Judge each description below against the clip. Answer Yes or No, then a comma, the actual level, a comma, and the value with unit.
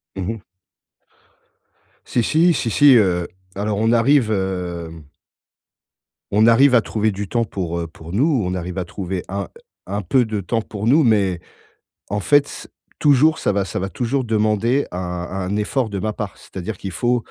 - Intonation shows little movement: No, average, 4.2 semitones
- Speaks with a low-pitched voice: Yes, low, 105 Hz